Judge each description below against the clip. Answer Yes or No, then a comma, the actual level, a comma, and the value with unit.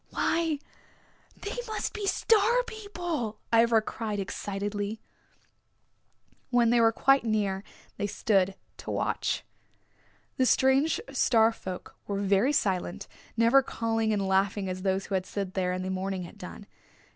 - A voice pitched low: No, high, 215 Hz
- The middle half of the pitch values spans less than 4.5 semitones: No, average, 5.2 semitones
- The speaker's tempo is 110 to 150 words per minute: Yes, average, 140 wpm